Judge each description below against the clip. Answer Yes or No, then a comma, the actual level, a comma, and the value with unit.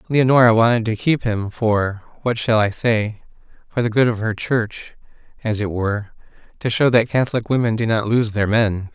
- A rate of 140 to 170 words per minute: No, average, 180 wpm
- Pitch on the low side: Yes, low, 110 Hz